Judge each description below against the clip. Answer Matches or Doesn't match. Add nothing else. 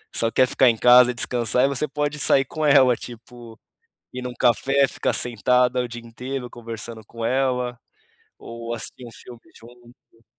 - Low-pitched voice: Matches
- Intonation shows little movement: Matches